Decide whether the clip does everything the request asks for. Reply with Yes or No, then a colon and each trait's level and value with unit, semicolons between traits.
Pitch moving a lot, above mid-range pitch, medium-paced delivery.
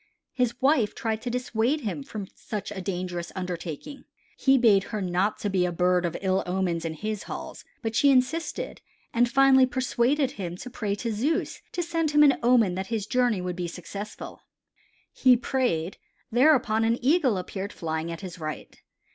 Yes: wide, 5.7 semitones; high, 215 Hz; average, 180 wpm